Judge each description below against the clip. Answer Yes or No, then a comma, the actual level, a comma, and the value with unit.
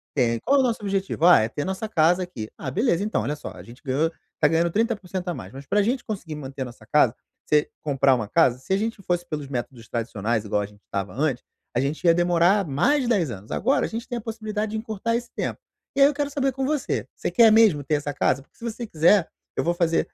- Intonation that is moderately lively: No, wide, 8.3 semitones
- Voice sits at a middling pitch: Yes, medium, 170 Hz